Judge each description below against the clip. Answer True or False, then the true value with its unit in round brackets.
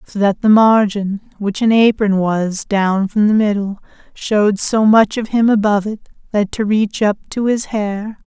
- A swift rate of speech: False (190 wpm)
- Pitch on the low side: False (210 Hz)